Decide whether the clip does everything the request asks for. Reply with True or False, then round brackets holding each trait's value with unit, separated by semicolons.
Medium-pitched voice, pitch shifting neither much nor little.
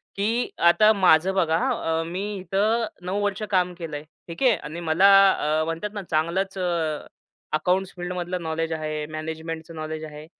True (170 Hz; 3.3 semitones)